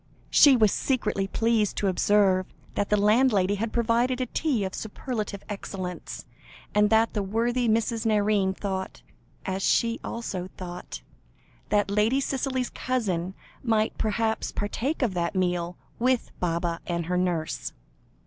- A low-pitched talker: No, high, 210 Hz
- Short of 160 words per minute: Yes, average, 140 wpm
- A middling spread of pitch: Yes, average, 3.7 semitones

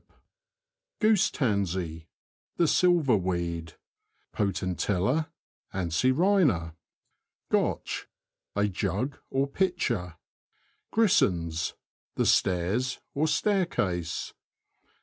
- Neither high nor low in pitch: No, low, 100 Hz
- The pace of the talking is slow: Yes, slow, 85 wpm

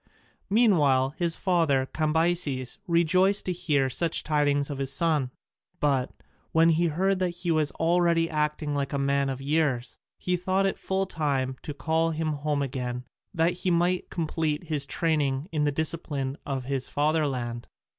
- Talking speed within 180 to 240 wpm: No, average, 160 wpm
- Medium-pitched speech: Yes, medium, 155 Hz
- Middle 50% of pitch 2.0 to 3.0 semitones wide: No, average, 3.5 semitones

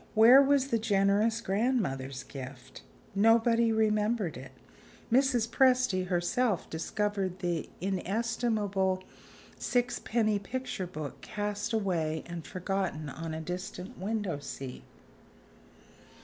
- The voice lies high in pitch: Yes, high, 200 Hz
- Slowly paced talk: Yes, slow, 100 wpm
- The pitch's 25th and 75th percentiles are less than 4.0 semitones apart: No, average, 4.6 semitones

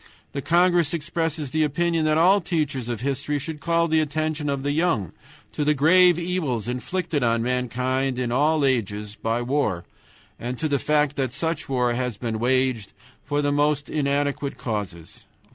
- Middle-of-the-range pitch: Yes, medium, 145 Hz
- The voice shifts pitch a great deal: No, average, 4.1 semitones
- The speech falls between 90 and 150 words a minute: No, average, 165 wpm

